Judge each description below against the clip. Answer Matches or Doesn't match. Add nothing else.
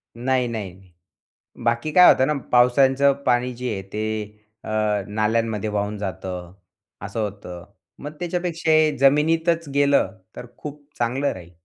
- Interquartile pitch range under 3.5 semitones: Doesn't match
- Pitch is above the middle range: Doesn't match